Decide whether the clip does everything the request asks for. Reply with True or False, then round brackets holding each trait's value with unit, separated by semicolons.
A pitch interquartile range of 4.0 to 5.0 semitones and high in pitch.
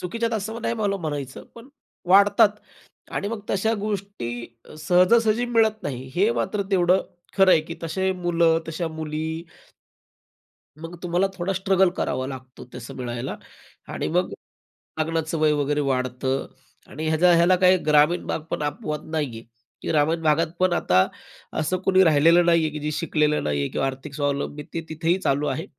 False (4.3 semitones; 165 Hz)